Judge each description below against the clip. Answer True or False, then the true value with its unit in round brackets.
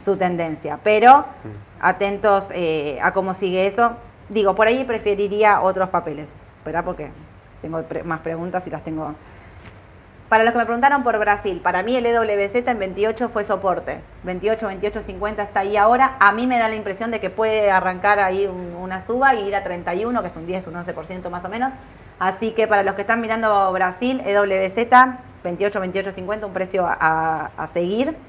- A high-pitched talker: True (195 Hz)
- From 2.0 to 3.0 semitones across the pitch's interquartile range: False (3.8 semitones)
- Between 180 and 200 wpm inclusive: True (190 wpm)